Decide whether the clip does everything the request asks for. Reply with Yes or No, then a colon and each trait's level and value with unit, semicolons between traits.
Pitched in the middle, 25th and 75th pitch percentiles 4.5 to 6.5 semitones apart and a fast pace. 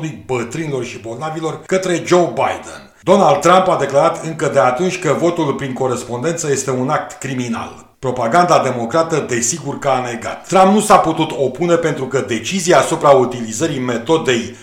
No: medium, 150 Hz; average, 5.1 semitones; average, 155 wpm